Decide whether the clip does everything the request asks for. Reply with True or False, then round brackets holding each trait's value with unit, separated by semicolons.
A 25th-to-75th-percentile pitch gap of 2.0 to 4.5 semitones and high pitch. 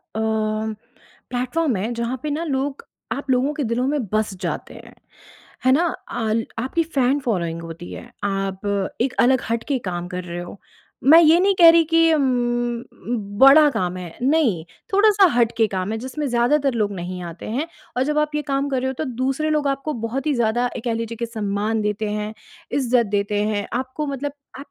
False (5.0 semitones; 245 Hz)